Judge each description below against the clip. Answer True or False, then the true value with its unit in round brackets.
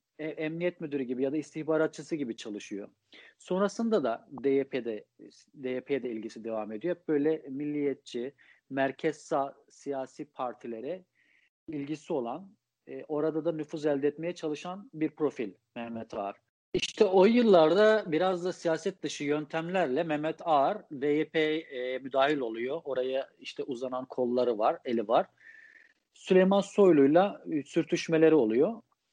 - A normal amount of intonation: True (4.5 semitones)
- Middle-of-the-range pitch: True (155 Hz)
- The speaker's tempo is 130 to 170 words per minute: False (115 wpm)